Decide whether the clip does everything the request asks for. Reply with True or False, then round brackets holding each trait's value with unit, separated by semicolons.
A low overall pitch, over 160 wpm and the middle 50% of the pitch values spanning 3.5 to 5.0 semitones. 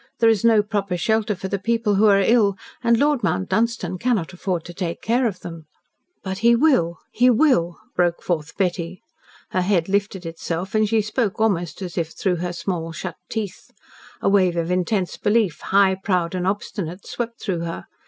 False (190 Hz; 190 wpm; 3.9 semitones)